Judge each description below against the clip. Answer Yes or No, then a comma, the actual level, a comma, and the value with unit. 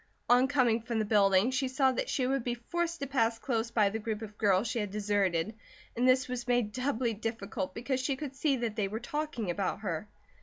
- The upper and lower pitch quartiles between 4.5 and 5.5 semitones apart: No, average, 3.6 semitones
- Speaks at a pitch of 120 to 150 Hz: No, high, 235 Hz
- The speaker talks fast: Yes, fast, 225 wpm